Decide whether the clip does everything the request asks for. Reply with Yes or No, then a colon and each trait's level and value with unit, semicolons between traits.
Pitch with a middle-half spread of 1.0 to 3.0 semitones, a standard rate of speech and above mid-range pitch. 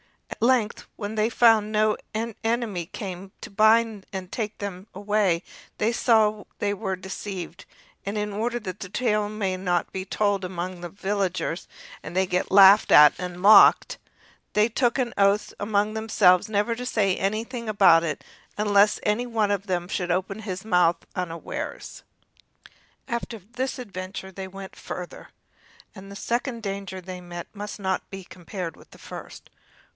Yes: average, 2.7 semitones; average, 165 wpm; high, 200 Hz